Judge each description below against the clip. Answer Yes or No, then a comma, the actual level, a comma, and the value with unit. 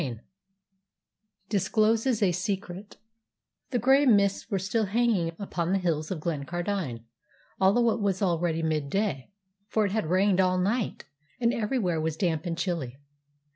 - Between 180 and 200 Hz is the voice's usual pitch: Yes, high, 190 Hz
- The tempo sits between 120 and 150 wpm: Yes, average, 145 wpm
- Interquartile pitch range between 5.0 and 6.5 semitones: No, average, 3.9 semitones